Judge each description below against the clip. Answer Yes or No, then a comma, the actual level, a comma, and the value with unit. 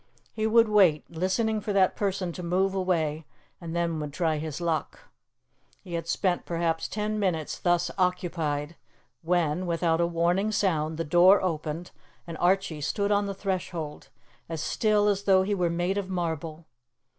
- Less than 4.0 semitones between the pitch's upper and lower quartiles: Yes, average, 3.0 semitones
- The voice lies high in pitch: No, medium, 175 Hz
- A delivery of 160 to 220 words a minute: Yes, average, 165 wpm